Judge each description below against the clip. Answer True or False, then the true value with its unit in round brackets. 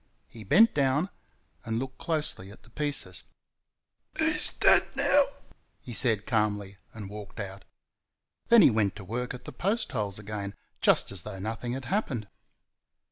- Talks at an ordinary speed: True (155 wpm)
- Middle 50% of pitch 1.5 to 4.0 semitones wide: False (4.7 semitones)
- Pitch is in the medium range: False (110 Hz)